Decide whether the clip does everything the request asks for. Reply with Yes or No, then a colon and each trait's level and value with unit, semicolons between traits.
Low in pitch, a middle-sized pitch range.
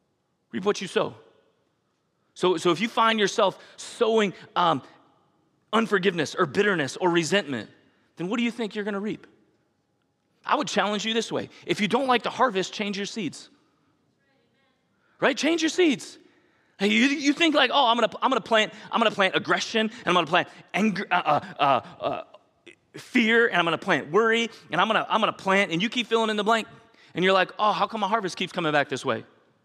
No: high, 205 Hz; average, 4.4 semitones